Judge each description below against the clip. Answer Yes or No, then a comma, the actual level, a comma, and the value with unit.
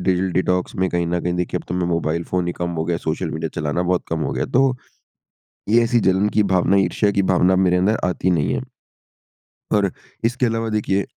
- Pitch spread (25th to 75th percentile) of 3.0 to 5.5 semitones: No, narrow, 2.6 semitones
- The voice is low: Yes, very low, 90 Hz